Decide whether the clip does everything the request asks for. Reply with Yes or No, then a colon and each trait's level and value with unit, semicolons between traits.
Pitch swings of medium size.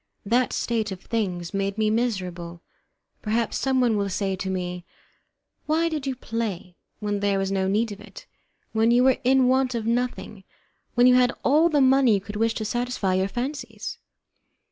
Yes: average, 4.3 semitones